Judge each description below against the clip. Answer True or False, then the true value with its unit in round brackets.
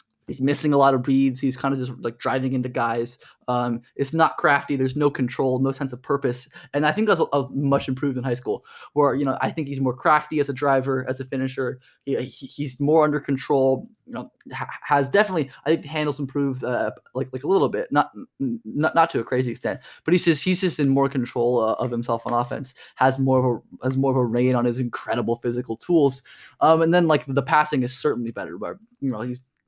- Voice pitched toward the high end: False (135 Hz)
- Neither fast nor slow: False (235 wpm)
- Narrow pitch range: True (2.3 semitones)